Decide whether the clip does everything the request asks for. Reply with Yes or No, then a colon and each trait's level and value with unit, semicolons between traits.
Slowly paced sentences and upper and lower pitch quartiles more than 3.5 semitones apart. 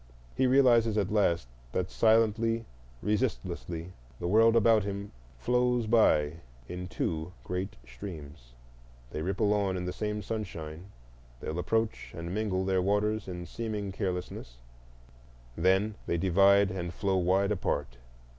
Yes: slow, 125 wpm; average, 4.4 semitones